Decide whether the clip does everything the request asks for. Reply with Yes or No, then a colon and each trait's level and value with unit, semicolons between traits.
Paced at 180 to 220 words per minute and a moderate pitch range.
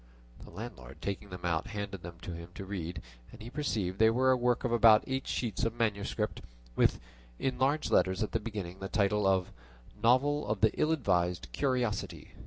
Yes: average, 195 wpm; average, 4.6 semitones